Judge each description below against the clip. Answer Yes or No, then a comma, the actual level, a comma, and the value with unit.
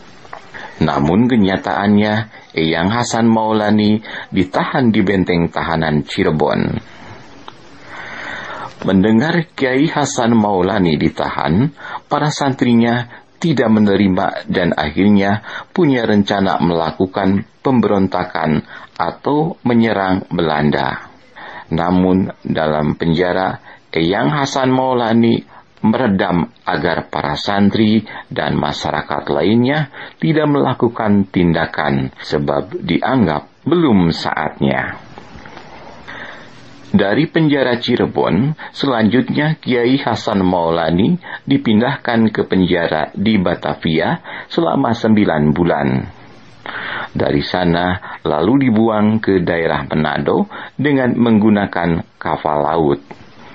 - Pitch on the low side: Yes, low, 100 Hz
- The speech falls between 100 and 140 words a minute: No, slow, 85 wpm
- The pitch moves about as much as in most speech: No, wide, 5.9 semitones